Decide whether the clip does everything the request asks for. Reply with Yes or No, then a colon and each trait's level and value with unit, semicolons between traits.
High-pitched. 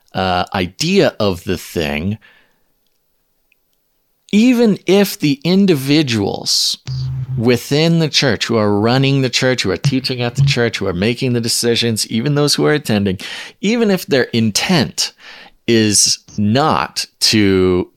No: low, 120 Hz